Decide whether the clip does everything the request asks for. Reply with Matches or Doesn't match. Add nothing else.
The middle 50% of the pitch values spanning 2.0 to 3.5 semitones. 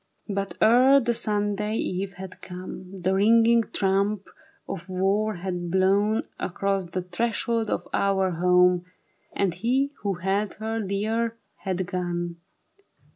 Matches